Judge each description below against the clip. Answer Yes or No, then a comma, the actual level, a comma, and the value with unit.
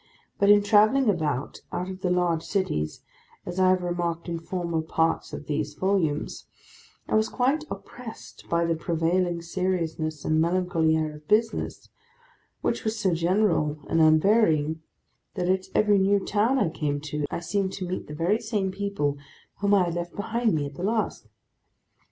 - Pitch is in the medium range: Yes, medium, 175 Hz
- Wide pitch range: No, average, 4.1 semitones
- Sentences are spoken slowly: No, average, 165 wpm